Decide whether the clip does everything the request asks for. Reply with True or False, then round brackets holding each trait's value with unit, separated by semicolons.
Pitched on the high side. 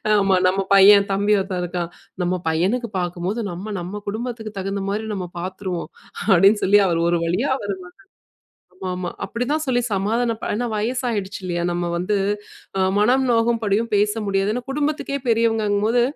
True (205 Hz)